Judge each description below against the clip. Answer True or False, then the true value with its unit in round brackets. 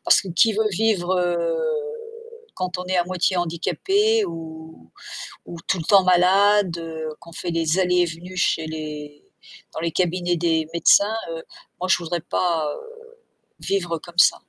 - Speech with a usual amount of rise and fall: False (2.1 semitones)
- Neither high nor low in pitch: True (175 Hz)